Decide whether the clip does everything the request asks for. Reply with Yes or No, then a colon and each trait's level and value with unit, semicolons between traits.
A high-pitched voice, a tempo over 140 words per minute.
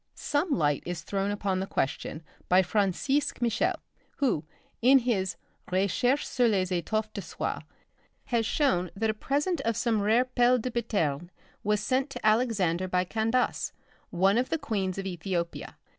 Yes: high, 210 Hz; average, 160 wpm